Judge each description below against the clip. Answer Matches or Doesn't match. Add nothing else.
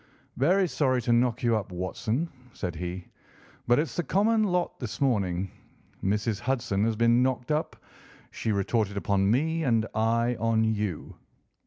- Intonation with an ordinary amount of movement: Matches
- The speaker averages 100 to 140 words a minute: Doesn't match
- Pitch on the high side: Doesn't match